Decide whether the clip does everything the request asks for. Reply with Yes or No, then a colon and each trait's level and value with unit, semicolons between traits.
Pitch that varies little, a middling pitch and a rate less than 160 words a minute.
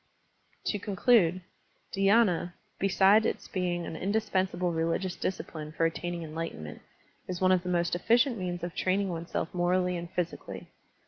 Yes: narrow, 2.2 semitones; medium, 180 Hz; average, 140 wpm